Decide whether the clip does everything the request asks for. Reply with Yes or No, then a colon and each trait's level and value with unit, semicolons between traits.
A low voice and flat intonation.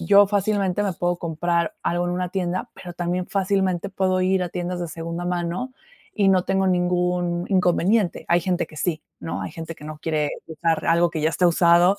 No: medium, 175 Hz; narrow, 1.7 semitones